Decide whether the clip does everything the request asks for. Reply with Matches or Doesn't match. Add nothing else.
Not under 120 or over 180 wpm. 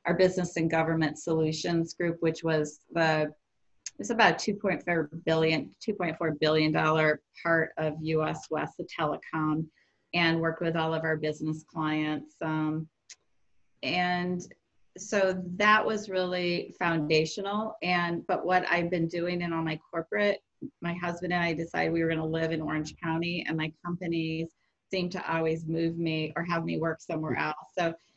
Matches